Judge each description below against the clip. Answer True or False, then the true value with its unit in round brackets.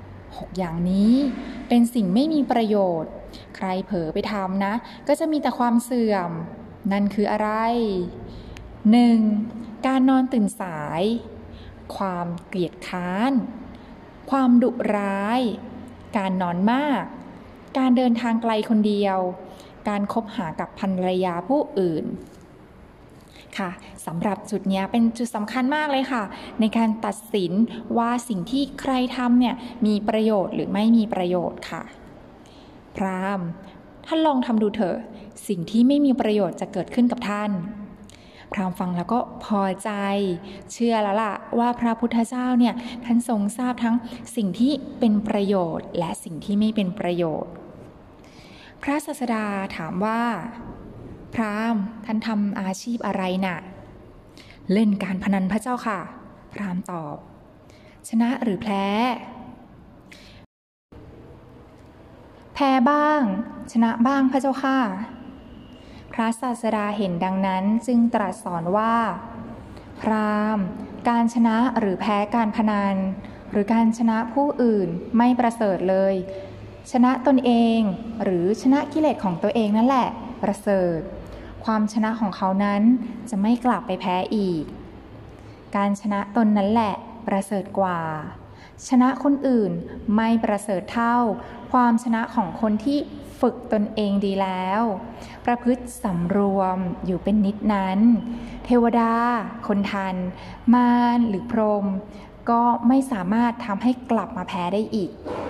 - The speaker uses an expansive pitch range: False (3.3 semitones)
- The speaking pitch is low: False (220 Hz)